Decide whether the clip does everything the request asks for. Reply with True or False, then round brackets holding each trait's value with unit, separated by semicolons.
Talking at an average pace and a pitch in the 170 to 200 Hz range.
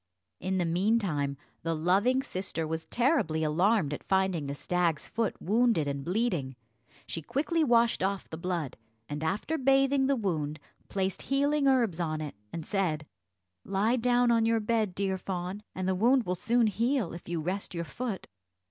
True (170 wpm; 190 Hz)